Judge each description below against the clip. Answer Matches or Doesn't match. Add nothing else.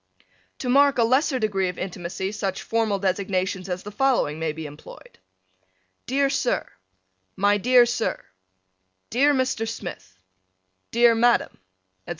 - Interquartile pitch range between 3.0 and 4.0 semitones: Doesn't match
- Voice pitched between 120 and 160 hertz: Doesn't match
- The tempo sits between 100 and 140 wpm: Matches